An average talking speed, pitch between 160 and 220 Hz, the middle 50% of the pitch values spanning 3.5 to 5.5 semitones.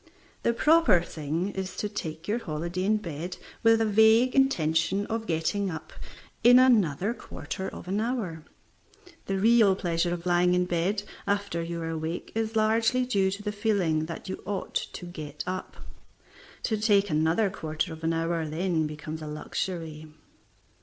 Yes: average, 165 wpm; medium, 185 Hz; average, 4.7 semitones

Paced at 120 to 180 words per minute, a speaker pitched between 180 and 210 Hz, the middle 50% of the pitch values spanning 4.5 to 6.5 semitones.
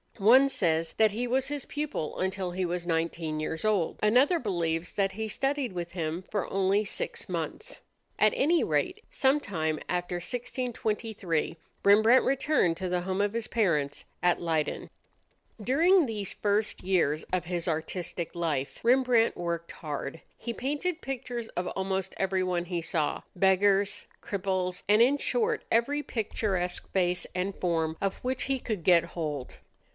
Yes: average, 150 wpm; high, 190 Hz; wide, 5.6 semitones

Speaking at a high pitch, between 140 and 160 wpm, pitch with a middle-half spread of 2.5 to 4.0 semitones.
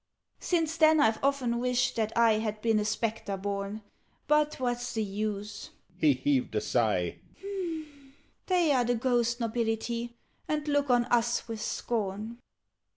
Yes: high, 230 Hz; average, 145 wpm; average, 3.0 semitones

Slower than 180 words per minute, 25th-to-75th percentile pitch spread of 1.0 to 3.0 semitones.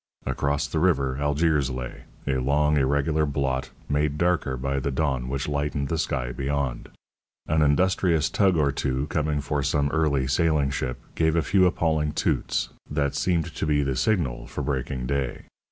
Yes: average, 170 wpm; narrow, 2.6 semitones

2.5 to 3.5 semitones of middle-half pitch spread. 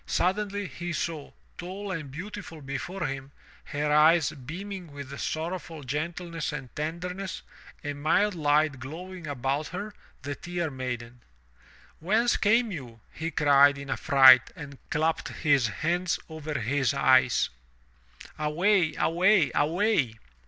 No: average, 4.2 semitones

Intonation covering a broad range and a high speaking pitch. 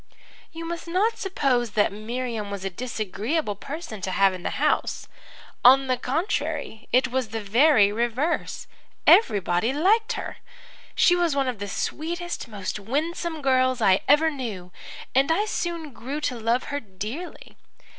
Yes: wide, 7.0 semitones; very high, 255 Hz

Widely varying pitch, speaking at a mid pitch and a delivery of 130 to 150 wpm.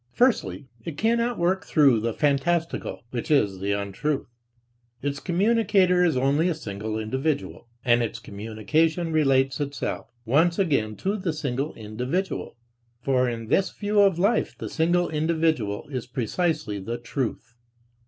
Yes: wide, 6.7 semitones; medium, 145 Hz; average, 140 wpm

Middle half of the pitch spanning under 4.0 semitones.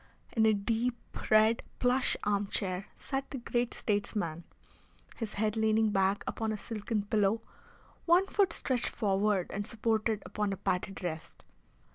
Yes: narrow, 2.4 semitones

